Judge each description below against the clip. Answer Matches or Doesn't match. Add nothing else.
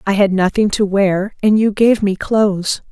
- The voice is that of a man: Doesn't match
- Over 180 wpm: Matches